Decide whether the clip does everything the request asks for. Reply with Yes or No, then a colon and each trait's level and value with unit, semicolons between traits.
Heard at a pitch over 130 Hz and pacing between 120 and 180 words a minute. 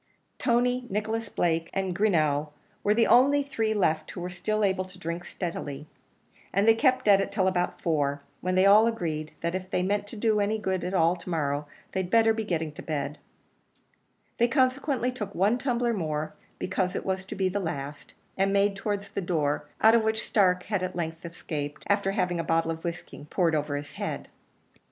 No: high, 190 Hz; average, 200 wpm